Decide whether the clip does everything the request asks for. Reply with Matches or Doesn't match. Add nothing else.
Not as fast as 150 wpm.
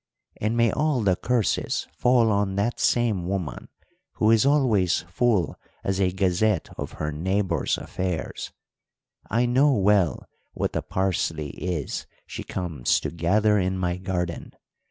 Matches